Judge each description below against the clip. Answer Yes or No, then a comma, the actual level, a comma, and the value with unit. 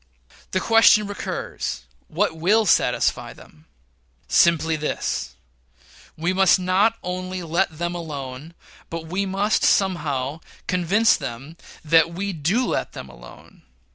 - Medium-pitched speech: Yes, medium, 175 Hz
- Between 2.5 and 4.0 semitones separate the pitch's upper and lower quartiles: Yes, average, 3.7 semitones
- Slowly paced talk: Yes, slow, 120 wpm